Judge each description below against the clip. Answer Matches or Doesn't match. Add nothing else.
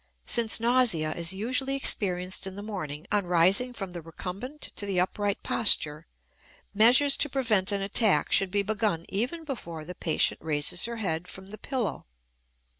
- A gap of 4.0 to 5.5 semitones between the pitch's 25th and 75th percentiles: Matches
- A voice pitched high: Matches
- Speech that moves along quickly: Doesn't match